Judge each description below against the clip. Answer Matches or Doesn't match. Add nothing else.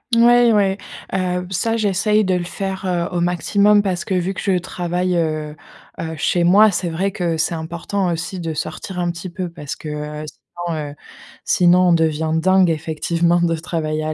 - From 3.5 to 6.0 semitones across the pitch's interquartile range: Doesn't match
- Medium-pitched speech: Matches